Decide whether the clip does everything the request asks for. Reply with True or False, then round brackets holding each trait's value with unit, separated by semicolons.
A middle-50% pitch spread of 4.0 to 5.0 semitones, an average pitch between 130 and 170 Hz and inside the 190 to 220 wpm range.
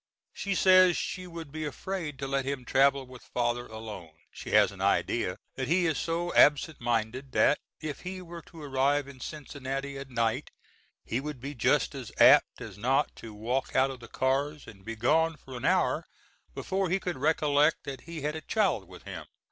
True (4.3 semitones; 140 Hz; 195 wpm)